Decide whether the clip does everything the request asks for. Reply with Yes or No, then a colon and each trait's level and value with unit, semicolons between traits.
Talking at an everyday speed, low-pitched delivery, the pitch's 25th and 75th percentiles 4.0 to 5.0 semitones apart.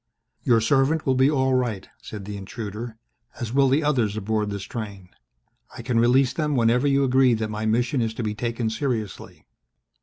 No: average, 185 wpm; low, 120 Hz; average, 3.4 semitones